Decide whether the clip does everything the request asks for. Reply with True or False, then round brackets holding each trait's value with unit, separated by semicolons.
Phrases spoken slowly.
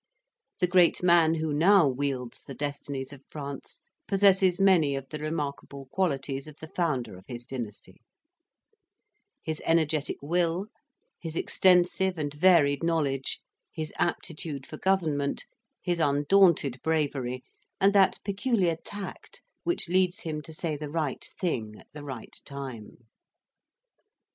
True (130 wpm)